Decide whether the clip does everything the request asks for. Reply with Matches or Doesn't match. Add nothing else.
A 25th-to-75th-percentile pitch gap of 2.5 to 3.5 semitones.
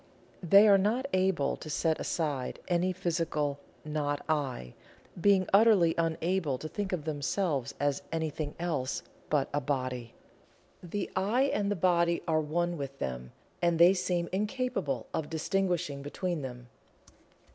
Doesn't match